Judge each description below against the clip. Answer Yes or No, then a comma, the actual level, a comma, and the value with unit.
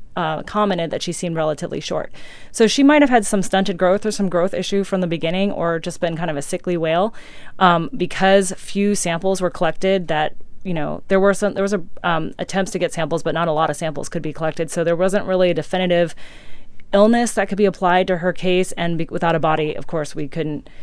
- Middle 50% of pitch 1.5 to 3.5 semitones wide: Yes, average, 2.8 semitones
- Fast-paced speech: Yes, fast, 235 wpm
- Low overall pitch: No, medium, 180 Hz